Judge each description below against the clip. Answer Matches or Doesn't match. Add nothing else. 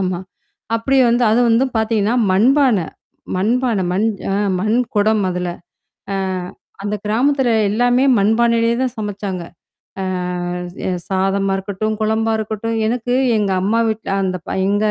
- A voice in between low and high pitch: Doesn't match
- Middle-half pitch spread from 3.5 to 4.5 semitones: Doesn't match